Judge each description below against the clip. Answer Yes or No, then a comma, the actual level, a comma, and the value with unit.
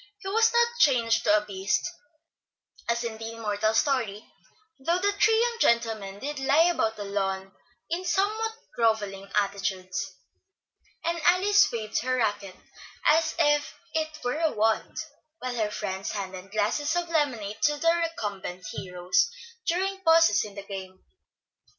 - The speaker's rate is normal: Yes, average, 145 wpm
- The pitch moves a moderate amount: No, wide, 8.5 semitones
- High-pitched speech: Yes, high, 235 Hz